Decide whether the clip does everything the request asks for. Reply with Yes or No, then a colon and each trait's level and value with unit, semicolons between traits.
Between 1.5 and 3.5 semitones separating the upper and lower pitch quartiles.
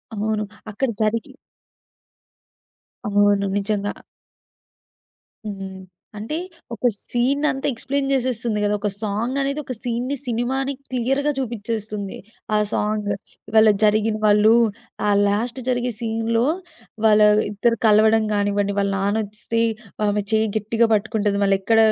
Yes: average, 2.8 semitones